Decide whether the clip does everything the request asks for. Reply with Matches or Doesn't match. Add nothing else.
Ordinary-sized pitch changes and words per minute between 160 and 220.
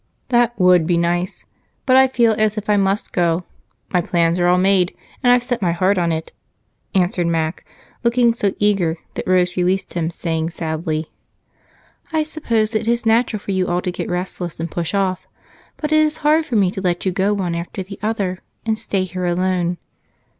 Matches